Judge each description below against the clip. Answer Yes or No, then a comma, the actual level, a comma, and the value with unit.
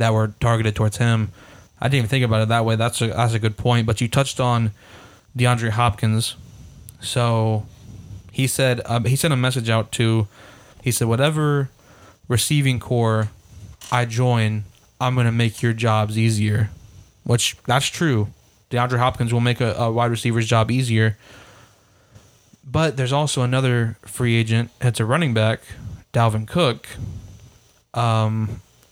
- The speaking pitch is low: Yes, low, 115 Hz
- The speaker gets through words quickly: No, average, 155 wpm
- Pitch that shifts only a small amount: Yes, narrow, 2.2 semitones